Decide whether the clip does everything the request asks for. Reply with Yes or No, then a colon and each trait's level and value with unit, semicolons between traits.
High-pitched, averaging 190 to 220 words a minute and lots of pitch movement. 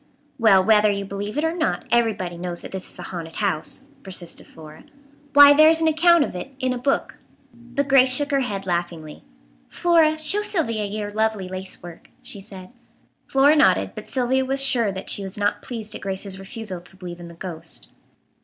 Yes: high, 210 Hz; average, 200 wpm; wide, 6.5 semitones